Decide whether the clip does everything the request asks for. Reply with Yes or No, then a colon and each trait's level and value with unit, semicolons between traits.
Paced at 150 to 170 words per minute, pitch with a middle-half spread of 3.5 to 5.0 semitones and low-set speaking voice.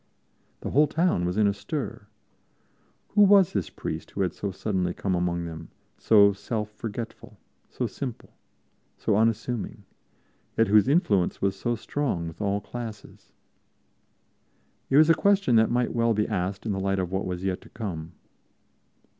Yes: average, 165 wpm; average, 4.0 semitones; low, 105 Hz